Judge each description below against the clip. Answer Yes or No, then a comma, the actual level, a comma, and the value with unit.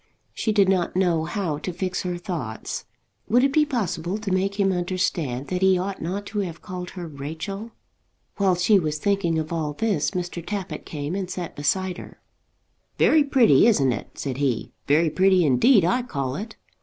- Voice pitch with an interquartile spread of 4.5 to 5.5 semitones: No, average, 3.8 semitones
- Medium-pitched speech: Yes, medium, 180 Hz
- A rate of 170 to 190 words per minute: Yes, average, 185 wpm